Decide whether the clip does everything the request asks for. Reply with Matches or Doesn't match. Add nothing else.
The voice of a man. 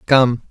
Matches